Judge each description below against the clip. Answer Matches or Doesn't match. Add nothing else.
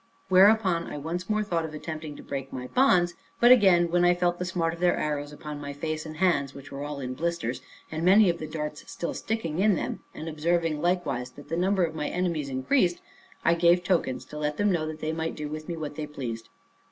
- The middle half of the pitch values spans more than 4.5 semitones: Doesn't match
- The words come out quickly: Matches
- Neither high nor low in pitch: Matches